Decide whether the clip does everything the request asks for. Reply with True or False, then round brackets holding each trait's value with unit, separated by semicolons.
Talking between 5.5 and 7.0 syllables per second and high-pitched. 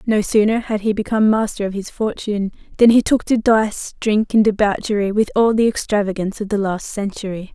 True (5.7 syllables/s; 210 Hz)